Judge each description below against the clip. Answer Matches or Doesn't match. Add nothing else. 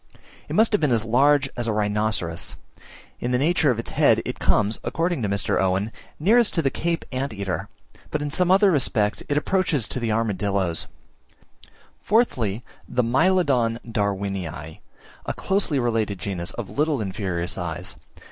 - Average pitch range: Doesn't match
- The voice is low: Matches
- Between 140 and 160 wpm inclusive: Matches